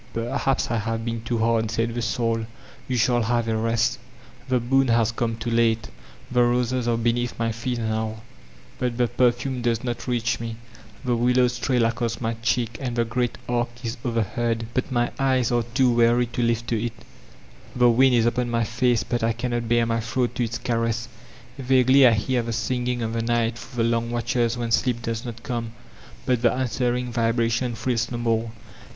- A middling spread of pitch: No, narrow, 1.2 semitones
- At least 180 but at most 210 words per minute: Yes, average, 200 wpm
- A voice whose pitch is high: No, low, 120 Hz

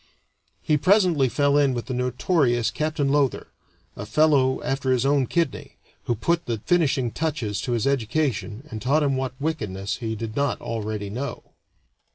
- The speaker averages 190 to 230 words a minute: No, average, 165 wpm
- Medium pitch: No, low, 130 Hz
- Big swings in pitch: No, average, 4.3 semitones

